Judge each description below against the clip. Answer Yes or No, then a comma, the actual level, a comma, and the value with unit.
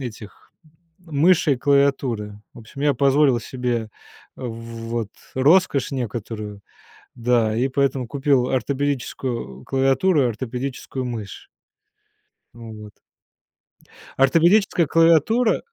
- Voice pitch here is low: Yes, low, 130 Hz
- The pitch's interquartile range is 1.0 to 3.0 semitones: No, average, 3.6 semitones